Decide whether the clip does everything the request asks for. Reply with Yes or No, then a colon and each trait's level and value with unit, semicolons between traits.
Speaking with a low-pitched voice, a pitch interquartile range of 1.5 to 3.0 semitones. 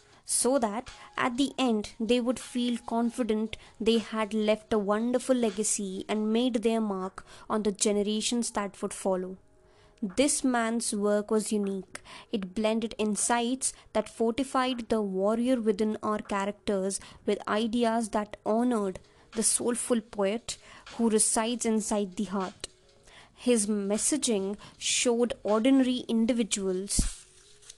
No: high, 220 Hz; narrow, 2.5 semitones